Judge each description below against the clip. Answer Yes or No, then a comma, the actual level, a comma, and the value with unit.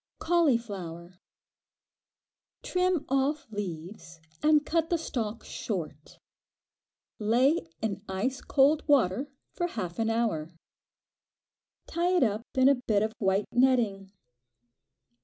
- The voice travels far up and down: Yes, wide, 6.7 semitones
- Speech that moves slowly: Yes, slow, 105 wpm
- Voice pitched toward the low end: No, high, 230 Hz